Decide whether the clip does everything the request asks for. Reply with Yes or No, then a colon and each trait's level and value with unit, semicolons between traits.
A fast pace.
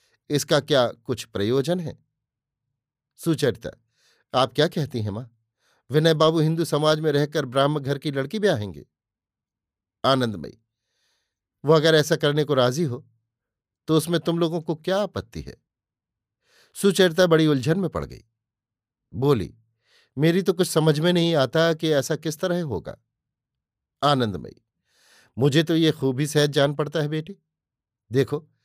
No: average, 145 wpm